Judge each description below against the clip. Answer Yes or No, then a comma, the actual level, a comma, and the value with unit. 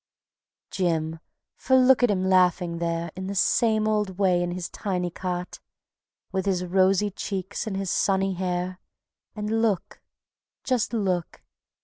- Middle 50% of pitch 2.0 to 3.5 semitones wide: Yes, narrow, 2.5 semitones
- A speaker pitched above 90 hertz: Yes, high, 190 Hz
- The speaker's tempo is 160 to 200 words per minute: No, average, 140 wpm